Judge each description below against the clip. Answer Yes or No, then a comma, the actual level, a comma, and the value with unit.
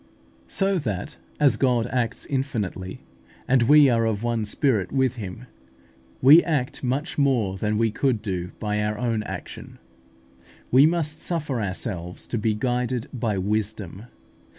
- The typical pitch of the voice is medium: No, low, 115 Hz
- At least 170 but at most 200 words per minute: No, average, 145 wpm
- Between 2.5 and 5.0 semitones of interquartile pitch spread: Yes, average, 4.2 semitones